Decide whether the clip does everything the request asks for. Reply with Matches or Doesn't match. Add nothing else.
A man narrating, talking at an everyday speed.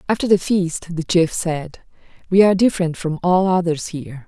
Doesn't match